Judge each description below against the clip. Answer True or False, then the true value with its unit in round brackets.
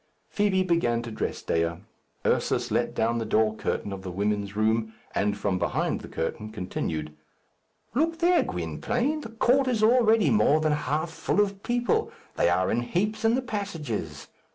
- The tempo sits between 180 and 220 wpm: False (170 wpm)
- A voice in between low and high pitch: True (145 Hz)